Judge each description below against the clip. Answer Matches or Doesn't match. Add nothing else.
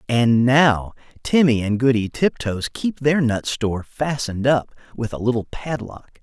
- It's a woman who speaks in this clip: Doesn't match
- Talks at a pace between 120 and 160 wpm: Matches